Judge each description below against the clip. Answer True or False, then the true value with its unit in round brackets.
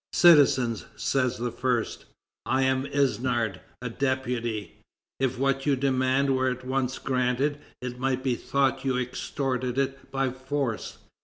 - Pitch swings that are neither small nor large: False (1.4 semitones)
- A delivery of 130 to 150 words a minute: True (140 wpm)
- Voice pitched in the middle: False (130 Hz)